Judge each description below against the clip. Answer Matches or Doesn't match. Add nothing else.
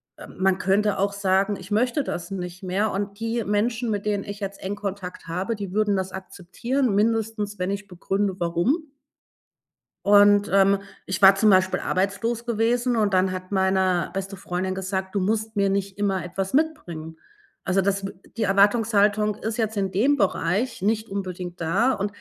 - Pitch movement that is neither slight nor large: Doesn't match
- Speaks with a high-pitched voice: Matches